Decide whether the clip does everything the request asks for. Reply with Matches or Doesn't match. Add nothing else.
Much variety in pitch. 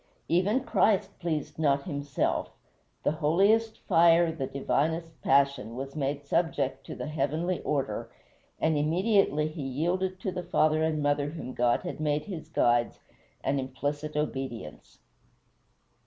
Doesn't match